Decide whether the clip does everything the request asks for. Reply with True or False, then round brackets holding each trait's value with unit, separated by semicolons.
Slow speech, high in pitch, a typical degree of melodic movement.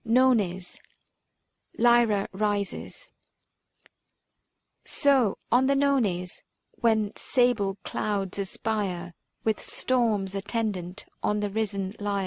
True (90 wpm; 210 Hz; 3.4 semitones)